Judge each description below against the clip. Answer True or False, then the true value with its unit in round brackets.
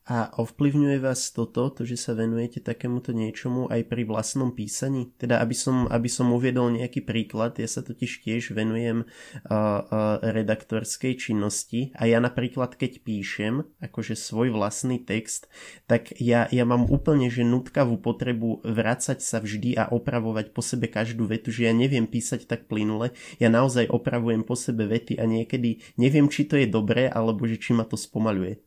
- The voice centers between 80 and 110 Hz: False (120 Hz)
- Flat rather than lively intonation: True (1.9 semitones)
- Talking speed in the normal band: False (170 wpm)